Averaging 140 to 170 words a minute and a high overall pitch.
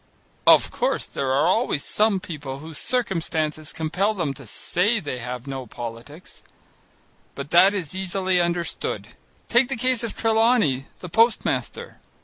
No: average, 145 wpm; medium, 170 Hz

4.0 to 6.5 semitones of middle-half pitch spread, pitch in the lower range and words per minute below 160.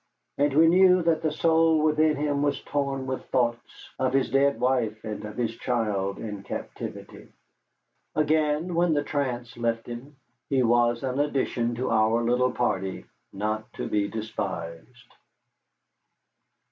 Yes: average, 4.3 semitones; low, 125 Hz; average, 145 wpm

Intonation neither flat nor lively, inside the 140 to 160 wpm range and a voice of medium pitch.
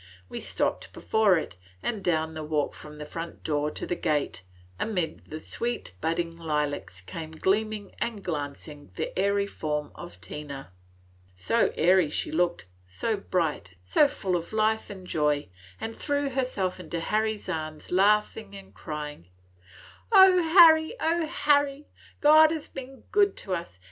No: wide, 6.8 semitones; average, 150 wpm; medium, 180 Hz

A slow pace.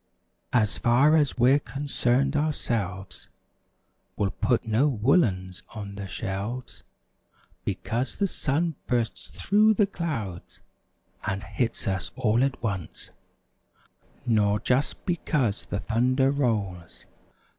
Yes: slow, 110 wpm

